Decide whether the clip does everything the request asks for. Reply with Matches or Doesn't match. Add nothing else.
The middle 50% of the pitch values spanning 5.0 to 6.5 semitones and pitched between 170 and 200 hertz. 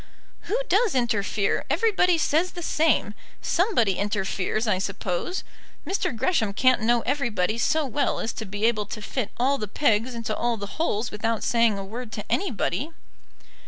Doesn't match